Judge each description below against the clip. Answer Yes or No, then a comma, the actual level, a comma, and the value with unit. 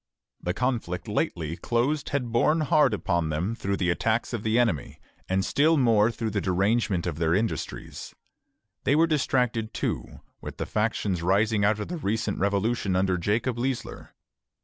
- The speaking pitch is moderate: No, low, 110 Hz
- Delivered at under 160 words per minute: No, average, 165 wpm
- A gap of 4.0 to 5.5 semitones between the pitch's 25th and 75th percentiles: Yes, average, 4.3 semitones